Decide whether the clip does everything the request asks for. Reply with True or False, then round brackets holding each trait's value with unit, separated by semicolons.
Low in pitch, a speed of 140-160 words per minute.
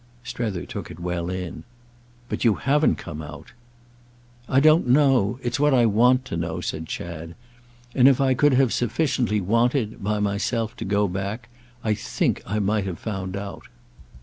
True (105 Hz; 155 wpm)